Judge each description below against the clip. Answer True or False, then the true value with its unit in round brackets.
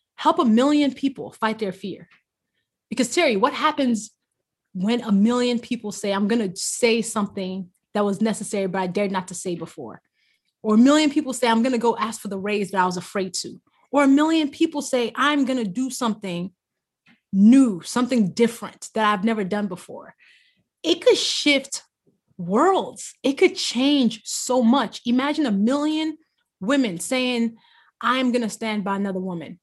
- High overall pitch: True (230 Hz)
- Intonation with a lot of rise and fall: False (4.7 semitones)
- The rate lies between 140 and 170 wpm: False (180 wpm)